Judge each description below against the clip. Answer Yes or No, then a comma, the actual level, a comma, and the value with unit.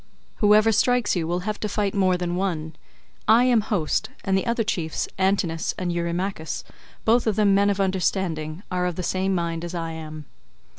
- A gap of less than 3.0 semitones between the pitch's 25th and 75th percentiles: No, average, 3.4 semitones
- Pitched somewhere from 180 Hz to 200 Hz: Yes, medium, 185 Hz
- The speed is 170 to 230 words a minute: Yes, average, 190 wpm